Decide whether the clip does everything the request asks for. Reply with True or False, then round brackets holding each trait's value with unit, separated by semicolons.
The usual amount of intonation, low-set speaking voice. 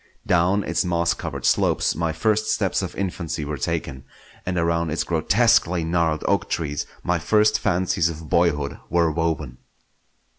False (2.2 semitones; 85 Hz)